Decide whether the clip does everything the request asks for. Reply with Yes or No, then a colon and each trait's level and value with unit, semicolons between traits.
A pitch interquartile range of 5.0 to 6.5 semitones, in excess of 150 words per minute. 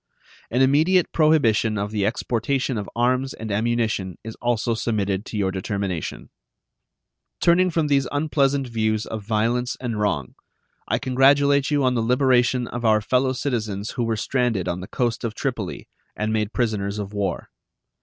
No: average, 3.8 semitones; average, 160 wpm